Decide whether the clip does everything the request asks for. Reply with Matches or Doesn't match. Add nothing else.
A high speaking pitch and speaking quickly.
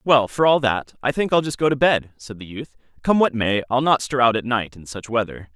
Doesn't match